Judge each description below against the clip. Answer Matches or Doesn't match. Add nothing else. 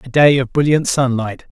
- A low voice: Matches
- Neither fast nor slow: Matches